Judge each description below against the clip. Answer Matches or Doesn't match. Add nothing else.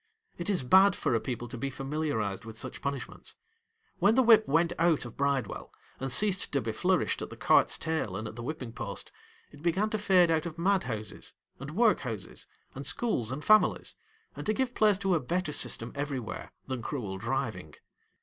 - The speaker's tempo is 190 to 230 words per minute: Matches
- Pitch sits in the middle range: Matches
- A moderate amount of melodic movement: Doesn't match